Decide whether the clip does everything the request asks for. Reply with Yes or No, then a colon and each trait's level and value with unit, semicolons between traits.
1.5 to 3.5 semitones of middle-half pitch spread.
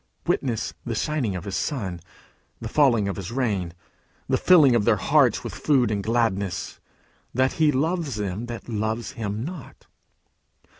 No: average, 4.8 semitones